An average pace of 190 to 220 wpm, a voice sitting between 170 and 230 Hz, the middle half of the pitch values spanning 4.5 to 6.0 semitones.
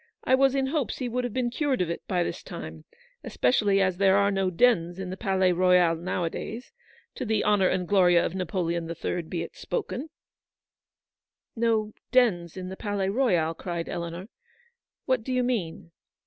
Yes: average, 195 wpm; high, 190 Hz; wide, 5.6 semitones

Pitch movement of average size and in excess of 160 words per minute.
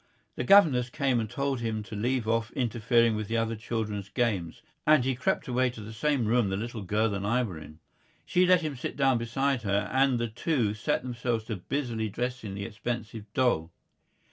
Yes: average, 3.0 semitones; average, 195 wpm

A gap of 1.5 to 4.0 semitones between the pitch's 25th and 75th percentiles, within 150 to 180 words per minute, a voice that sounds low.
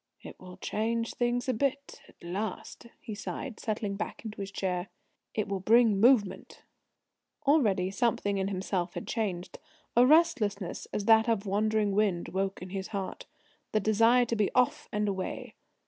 No: average, 3.1 semitones; average, 165 wpm; high, 210 Hz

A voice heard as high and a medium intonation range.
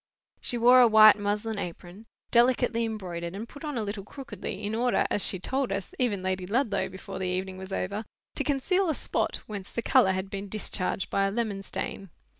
Yes: high, 205 Hz; average, 3.7 semitones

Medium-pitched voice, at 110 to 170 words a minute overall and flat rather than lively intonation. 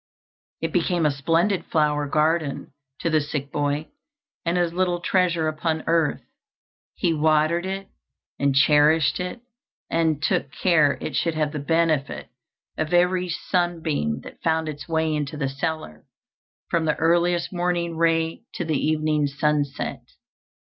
Yes: medium, 160 Hz; average, 140 wpm; narrow, 2.3 semitones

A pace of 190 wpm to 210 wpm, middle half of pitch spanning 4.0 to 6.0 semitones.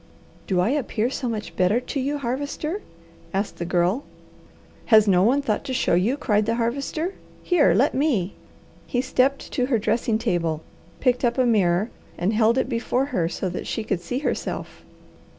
No: average, 180 wpm; average, 5.2 semitones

